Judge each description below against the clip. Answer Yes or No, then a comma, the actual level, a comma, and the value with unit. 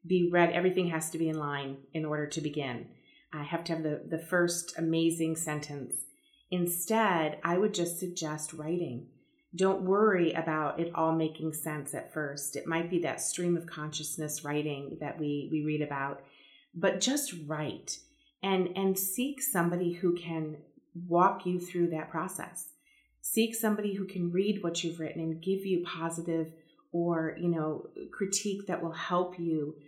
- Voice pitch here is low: No, medium, 165 Hz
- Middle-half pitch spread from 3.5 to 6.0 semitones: No, average, 2.9 semitones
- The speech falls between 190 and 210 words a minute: No, average, 165 wpm